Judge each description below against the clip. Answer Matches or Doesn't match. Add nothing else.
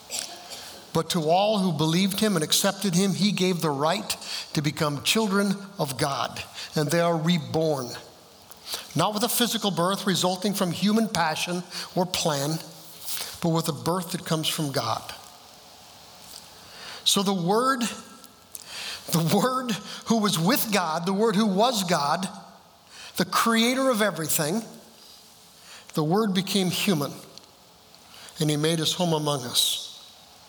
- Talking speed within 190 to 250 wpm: Doesn't match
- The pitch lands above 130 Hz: Matches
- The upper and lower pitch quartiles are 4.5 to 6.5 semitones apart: Matches